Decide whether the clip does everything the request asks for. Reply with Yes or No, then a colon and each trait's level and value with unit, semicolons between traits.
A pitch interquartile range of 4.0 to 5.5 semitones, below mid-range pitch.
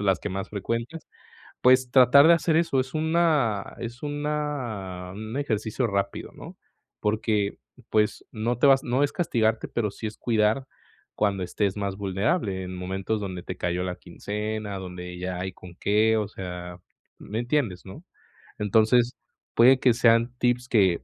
Yes: average, 4.5 semitones; low, 110 Hz